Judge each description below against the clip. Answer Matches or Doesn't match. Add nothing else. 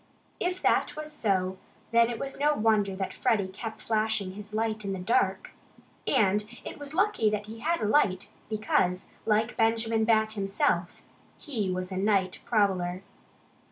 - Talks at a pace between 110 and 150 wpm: Doesn't match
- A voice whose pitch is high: Matches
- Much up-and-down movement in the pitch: Doesn't match